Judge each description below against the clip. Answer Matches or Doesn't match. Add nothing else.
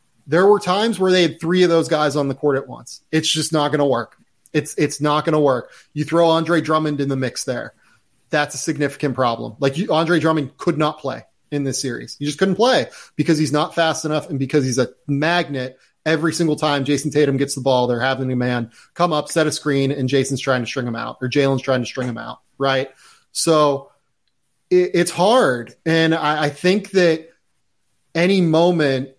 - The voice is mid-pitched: Matches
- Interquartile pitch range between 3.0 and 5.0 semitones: Matches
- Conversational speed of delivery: Doesn't match